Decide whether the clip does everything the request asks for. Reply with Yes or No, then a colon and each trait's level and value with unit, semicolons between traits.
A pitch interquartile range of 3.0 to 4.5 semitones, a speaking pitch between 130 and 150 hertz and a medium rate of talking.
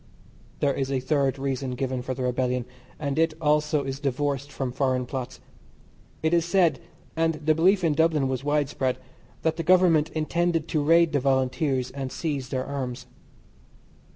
Yes: average, 3.4 semitones; medium, 140 Hz; average, 165 wpm